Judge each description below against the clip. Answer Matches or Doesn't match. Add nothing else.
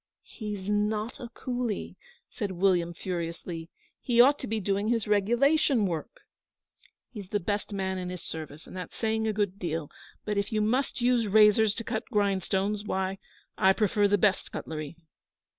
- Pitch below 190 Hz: Doesn't match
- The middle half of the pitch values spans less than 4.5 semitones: Matches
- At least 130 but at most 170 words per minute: Matches